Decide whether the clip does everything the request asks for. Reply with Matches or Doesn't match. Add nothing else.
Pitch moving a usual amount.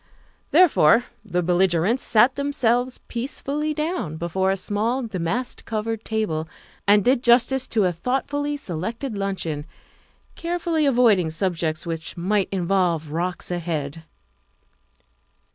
Doesn't match